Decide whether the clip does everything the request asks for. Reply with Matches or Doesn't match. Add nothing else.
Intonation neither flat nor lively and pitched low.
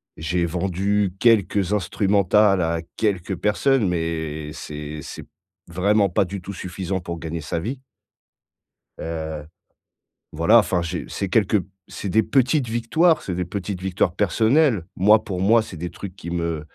Matches